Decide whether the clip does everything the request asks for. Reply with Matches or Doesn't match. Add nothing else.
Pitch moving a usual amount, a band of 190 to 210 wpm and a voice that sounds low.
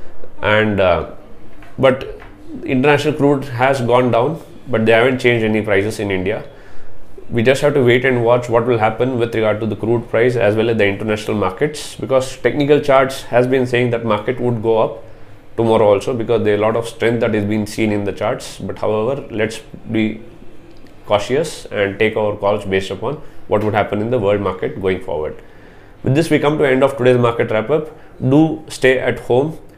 Matches